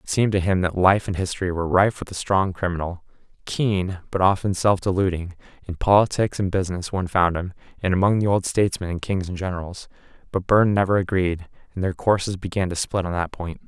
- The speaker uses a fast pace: Yes, fast, 210 wpm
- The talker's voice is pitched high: No, very low, 95 Hz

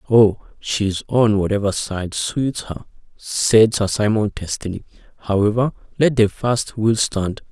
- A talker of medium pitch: No, low, 110 Hz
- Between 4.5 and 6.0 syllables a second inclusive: No, 4.0 syllables/s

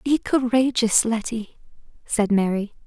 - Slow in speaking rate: Yes, slow, 105 wpm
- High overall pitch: Yes, high, 230 Hz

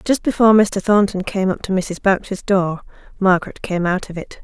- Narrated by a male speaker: No, female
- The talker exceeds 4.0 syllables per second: Yes, 5.3 syllables/s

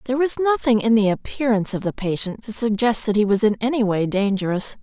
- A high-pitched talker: Yes, high, 220 Hz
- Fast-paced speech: Yes, fast, 225 wpm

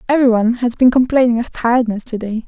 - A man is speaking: No, female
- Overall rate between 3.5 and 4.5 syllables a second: No, 7.0 syllables/s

